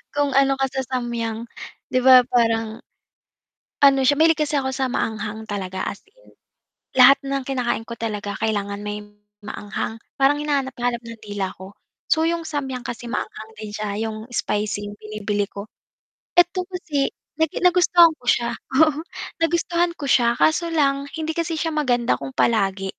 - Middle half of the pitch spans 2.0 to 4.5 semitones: No, wide, 5.5 semitones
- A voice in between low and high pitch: No, very high, 250 Hz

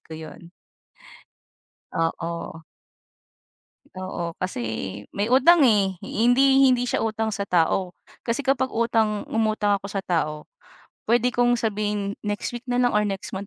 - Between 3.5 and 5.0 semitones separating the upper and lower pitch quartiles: Yes, average, 4.1 semitones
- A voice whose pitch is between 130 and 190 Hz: No, high, 210 Hz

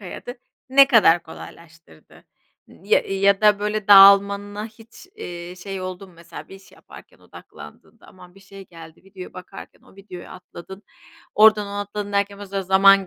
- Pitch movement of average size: No, narrow, 2.0 semitones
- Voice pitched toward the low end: No, high, 195 Hz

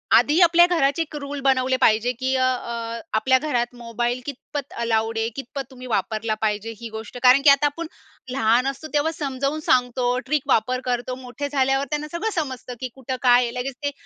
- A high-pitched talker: Yes, very high, 255 Hz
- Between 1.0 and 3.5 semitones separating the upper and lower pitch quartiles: Yes, average, 3.0 semitones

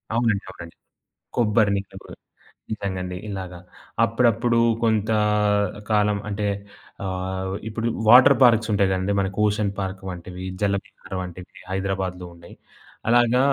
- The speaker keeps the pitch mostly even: No, average, 3.0 semitones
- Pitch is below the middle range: Yes, low, 100 Hz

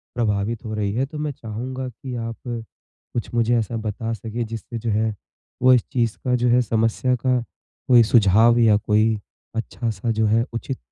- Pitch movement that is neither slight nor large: No, narrow, 1.9 semitones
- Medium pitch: No, low, 115 Hz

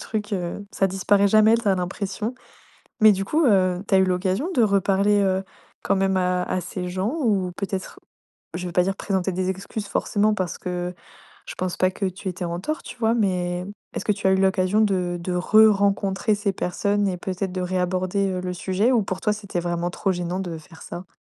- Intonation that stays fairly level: Yes, narrow, 2.1 semitones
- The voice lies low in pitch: No, high, 190 Hz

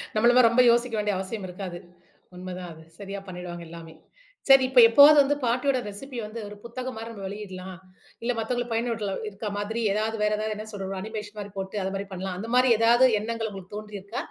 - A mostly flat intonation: No, average, 3.4 semitones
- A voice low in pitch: No, high, 210 Hz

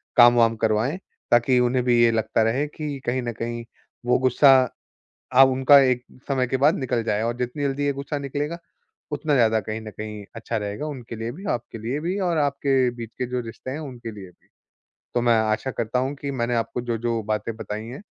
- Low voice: Yes, low, 125 Hz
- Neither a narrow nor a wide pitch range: Yes, average, 3.4 semitones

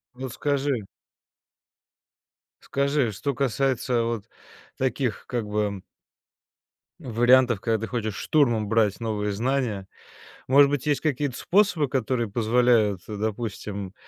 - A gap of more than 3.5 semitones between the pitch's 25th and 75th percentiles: Yes, average, 4.0 semitones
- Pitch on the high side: No, low, 120 Hz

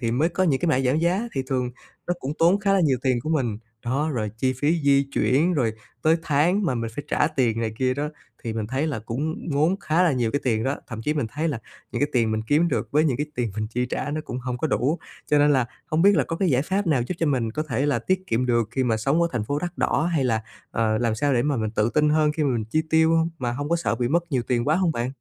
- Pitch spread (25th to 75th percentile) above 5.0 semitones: No, average, 4.7 semitones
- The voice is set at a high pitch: No, medium, 140 Hz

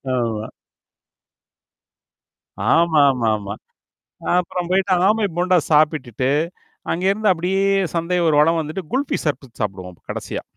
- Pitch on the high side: No, medium, 160 Hz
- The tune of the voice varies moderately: No, wide, 6.7 semitones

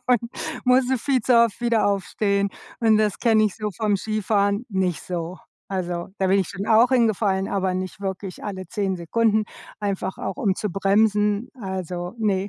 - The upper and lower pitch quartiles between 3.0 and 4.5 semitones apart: No, narrow, 2.5 semitones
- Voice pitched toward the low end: No, high, 200 Hz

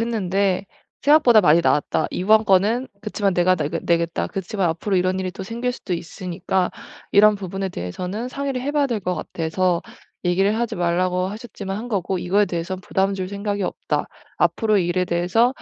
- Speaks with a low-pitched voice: No, high, 190 Hz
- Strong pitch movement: No, average, 3.1 semitones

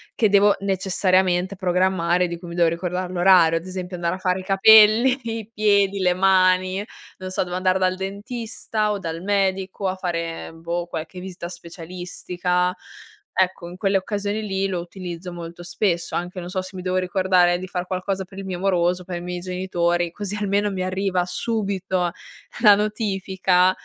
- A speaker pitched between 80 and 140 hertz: No, medium, 185 Hz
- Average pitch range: No, narrow, 1.7 semitones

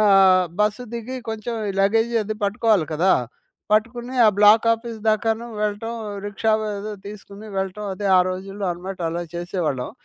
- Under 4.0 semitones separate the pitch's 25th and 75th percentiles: Yes, narrow, 2.5 semitones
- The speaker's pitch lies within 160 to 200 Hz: No, high, 210 Hz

